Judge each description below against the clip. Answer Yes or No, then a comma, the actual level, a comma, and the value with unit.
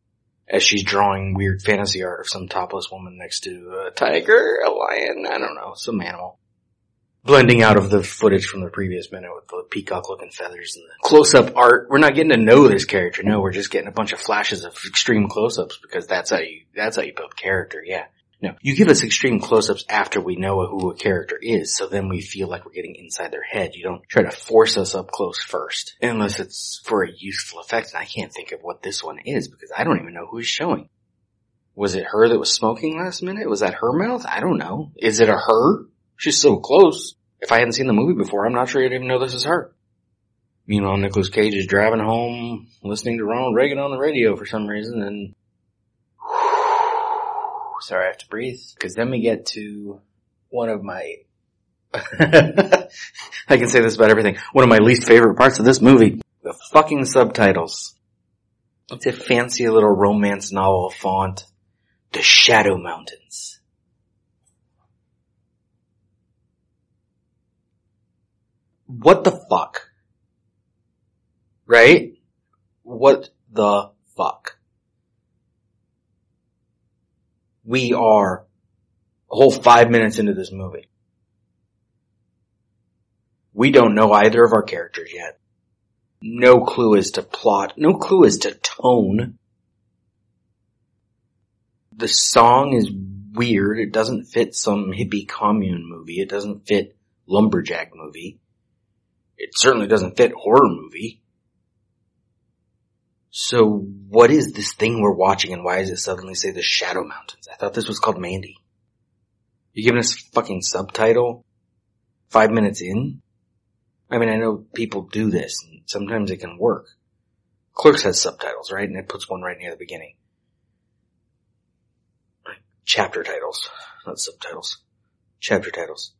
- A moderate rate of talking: Yes, average, 160 wpm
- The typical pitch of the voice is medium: No, low, 110 Hz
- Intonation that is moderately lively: Yes, average, 4.4 semitones